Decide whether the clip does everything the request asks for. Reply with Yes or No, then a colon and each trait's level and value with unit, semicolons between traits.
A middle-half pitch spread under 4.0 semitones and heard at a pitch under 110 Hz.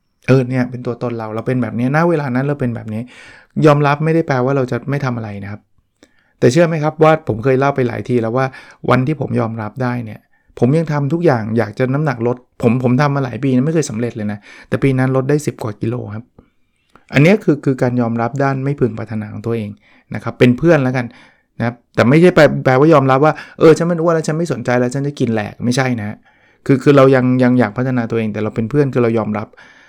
No: average, 3.4 semitones; low, 125 Hz